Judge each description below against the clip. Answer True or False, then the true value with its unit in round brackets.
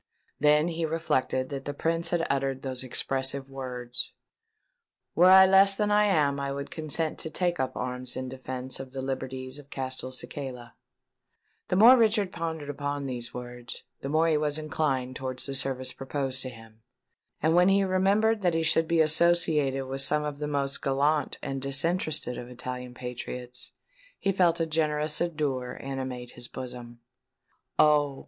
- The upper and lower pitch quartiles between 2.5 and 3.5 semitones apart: False (3.9 semitones)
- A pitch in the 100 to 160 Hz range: True (140 Hz)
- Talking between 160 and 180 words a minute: True (165 wpm)